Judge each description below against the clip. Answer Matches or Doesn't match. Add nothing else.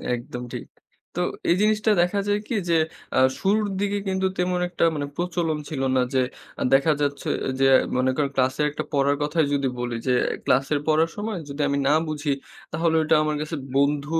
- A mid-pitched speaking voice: Matches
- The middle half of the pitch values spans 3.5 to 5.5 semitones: Matches